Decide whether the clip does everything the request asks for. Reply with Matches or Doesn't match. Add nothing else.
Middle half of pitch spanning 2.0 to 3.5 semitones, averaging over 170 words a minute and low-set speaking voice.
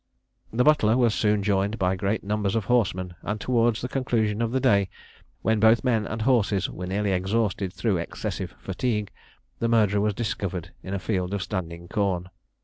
Matches